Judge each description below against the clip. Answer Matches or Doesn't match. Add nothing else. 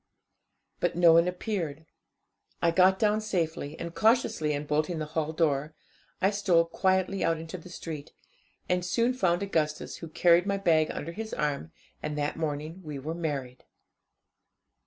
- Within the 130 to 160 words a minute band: Matches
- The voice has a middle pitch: Matches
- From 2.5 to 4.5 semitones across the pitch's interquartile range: Matches